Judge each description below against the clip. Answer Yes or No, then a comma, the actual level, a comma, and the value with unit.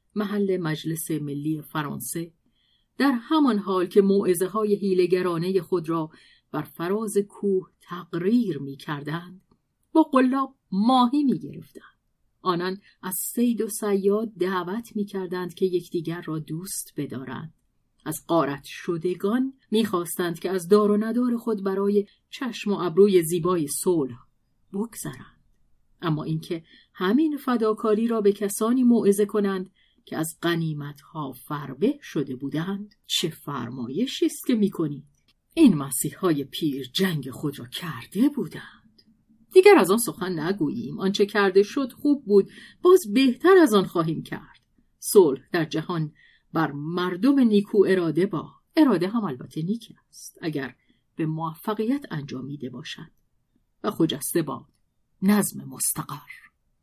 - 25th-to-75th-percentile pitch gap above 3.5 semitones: Yes, average, 5.2 semitones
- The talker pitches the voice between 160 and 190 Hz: Yes, medium, 185 Hz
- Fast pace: No, average, 130 wpm